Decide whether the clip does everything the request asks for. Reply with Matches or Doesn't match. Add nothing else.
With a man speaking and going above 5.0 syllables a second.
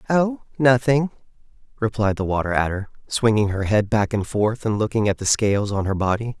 Matches